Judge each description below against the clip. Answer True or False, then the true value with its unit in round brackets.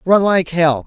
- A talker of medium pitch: True (170 Hz)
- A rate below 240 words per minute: True (210 wpm)